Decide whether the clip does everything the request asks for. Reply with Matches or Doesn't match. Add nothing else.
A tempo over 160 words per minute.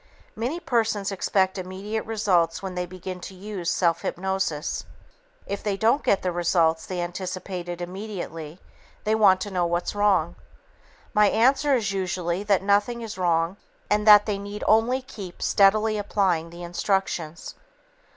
Doesn't match